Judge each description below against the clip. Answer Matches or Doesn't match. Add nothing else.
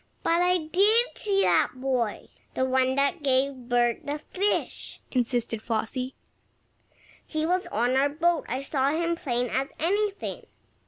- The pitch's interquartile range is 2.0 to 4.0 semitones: Doesn't match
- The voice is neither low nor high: Doesn't match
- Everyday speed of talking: Matches